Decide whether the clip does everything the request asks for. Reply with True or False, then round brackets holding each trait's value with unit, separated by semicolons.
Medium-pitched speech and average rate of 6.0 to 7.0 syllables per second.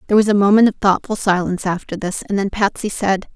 False (200 Hz; 6.4 syllables/s)